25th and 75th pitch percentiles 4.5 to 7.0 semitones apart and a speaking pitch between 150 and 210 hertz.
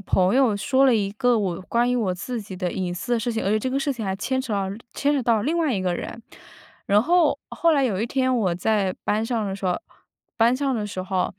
No: average, 4.9 semitones; high, 225 Hz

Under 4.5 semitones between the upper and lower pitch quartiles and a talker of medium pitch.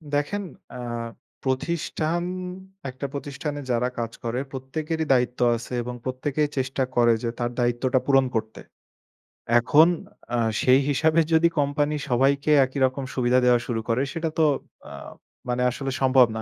No: average, 3.0 semitones; low, 130 Hz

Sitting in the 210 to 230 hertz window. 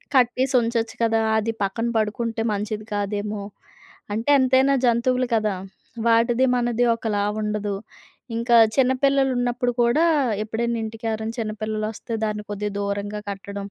Yes: high, 225 Hz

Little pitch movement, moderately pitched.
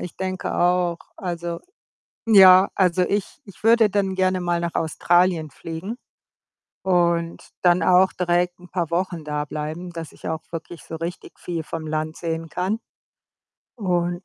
Yes: narrow, 2.0 semitones; medium, 175 Hz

